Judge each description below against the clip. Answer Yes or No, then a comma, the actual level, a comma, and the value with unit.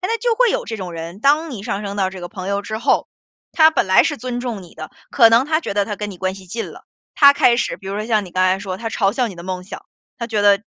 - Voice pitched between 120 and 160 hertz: No, high, 205 Hz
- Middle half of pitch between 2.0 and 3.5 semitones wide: No, average, 4.5 semitones